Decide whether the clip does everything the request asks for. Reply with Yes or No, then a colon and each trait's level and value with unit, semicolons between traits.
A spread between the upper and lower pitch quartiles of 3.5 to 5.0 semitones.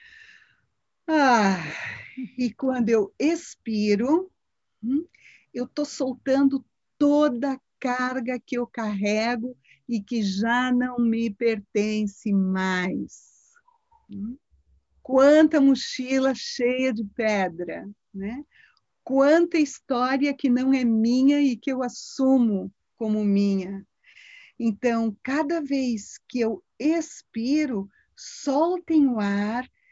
Yes: average, 4.4 semitones